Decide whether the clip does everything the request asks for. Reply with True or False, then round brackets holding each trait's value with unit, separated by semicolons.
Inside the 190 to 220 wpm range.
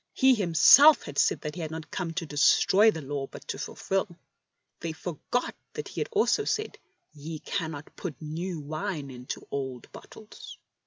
False (175 wpm)